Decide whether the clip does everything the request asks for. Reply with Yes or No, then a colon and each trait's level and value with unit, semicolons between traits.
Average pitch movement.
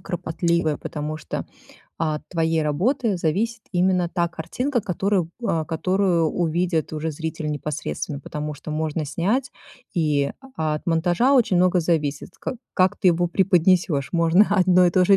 Yes: average, 3.0 semitones